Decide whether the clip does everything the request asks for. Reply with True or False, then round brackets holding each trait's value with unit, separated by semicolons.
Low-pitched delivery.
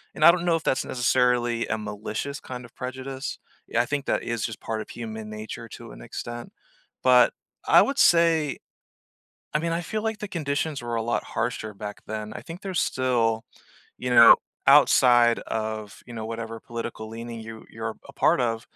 True (120 Hz)